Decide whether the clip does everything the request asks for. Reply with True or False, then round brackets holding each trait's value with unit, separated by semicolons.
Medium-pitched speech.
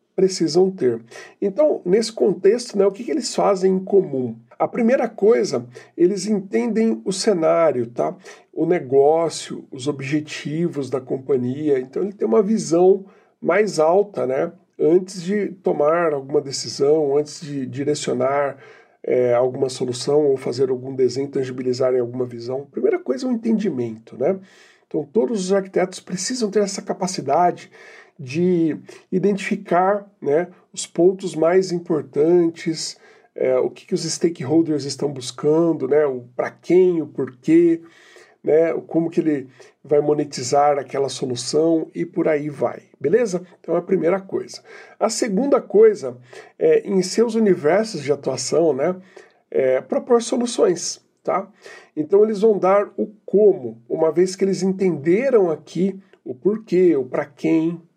True (175 Hz)